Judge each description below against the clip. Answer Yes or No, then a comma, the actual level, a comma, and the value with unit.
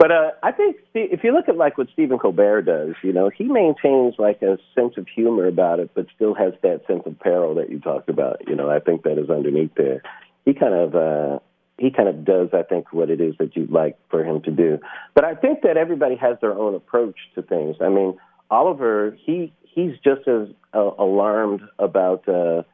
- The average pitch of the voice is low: Yes, low, 105 Hz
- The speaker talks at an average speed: No, fast, 225 wpm